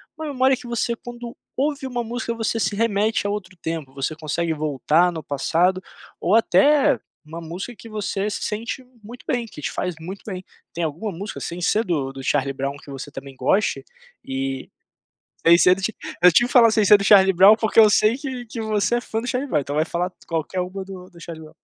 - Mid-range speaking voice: No, high, 195 Hz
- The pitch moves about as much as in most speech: No, wide, 5.9 semitones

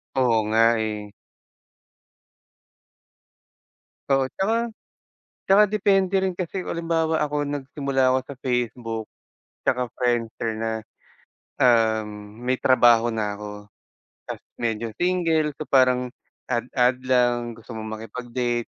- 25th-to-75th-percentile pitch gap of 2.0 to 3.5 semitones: No, average, 4.4 semitones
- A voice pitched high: No, low, 125 Hz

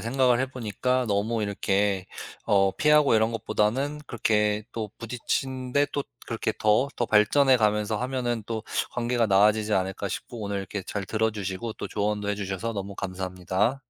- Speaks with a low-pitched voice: Yes, low, 110 Hz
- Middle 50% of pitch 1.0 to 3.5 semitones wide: Yes, average, 3.2 semitones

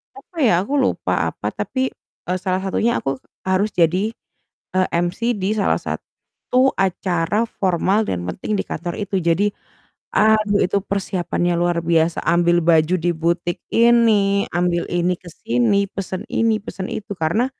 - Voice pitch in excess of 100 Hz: Yes, medium, 185 Hz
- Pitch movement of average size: Yes, average, 3.3 semitones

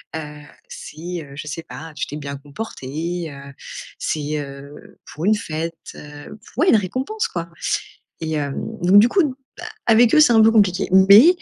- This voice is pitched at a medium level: Yes, medium, 165 Hz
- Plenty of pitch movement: Yes, wide, 6.2 semitones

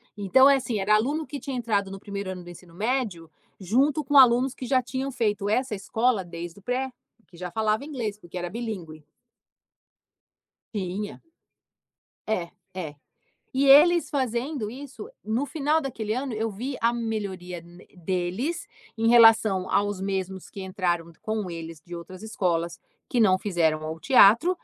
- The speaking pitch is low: No, high, 215 Hz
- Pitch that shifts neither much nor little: No, wide, 5.7 semitones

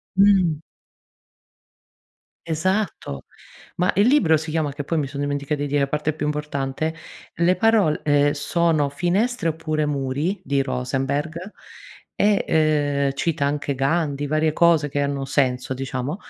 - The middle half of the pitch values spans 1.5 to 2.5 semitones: No, average, 2.9 semitones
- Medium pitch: Yes, medium, 150 Hz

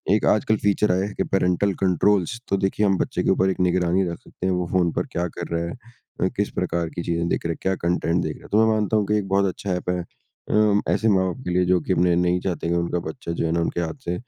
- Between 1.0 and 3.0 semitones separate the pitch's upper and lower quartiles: Yes, narrow, 2.4 semitones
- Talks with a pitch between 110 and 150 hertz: No, very low, 90 Hz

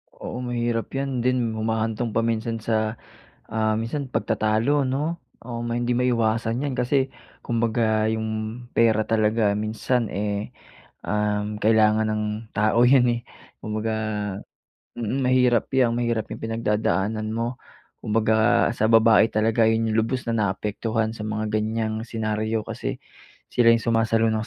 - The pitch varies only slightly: Yes, narrow, 1.6 semitones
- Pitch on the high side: No, low, 115 Hz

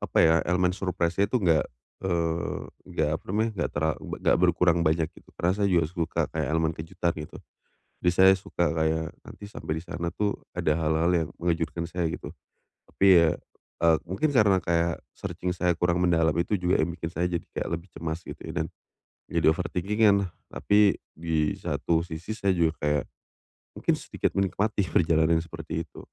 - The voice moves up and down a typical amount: No, narrow, 2.3 semitones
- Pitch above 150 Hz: No, very low, 85 Hz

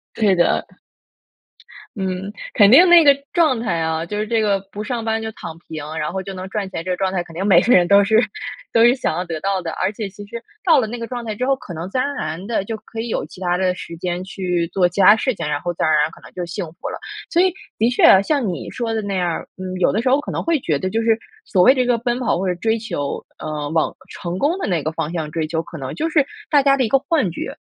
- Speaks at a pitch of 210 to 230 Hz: No, high, 200 Hz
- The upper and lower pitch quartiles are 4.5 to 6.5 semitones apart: Yes, average, 5.1 semitones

